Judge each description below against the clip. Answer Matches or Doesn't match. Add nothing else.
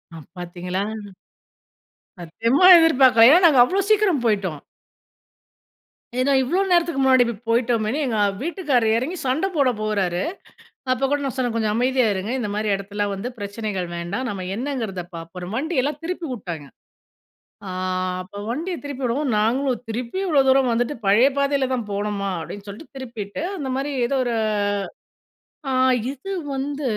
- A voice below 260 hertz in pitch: Matches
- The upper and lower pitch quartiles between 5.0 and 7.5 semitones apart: Matches